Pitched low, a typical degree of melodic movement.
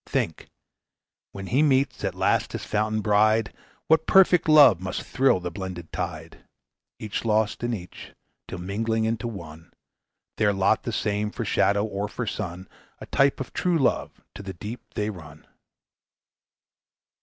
Yes: low, 105 Hz; average, 3.6 semitones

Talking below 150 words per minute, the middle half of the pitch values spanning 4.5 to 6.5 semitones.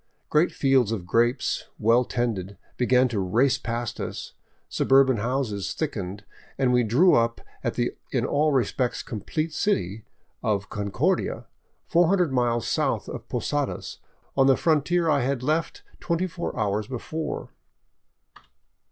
Yes: average, 140 wpm; average, 5.2 semitones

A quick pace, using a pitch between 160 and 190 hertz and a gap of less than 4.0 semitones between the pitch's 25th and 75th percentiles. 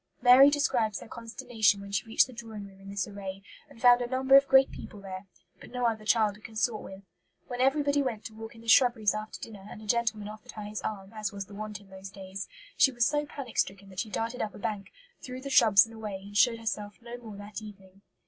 No: fast, 245 wpm; high, 215 Hz; average, 3.3 semitones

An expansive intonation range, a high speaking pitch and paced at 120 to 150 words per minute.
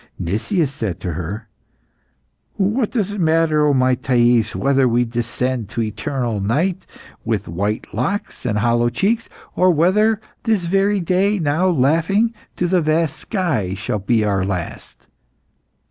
No: wide, 8.7 semitones; low, 135 Hz; average, 145 wpm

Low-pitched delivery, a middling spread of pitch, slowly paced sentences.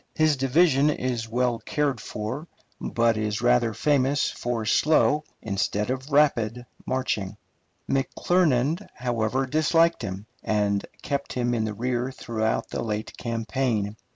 Yes: low, 125 Hz; average, 4.2 semitones; slow, 125 wpm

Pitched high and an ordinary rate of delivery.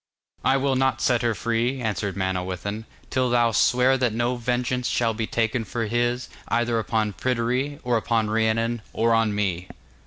No: low, 115 Hz; average, 165 wpm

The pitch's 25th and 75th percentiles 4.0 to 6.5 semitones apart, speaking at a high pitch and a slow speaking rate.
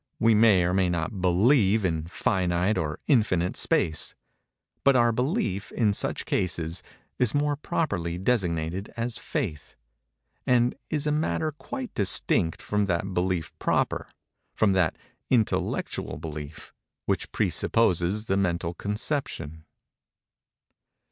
No: wide, 5.5 semitones; very low, 95 Hz; slow, 115 wpm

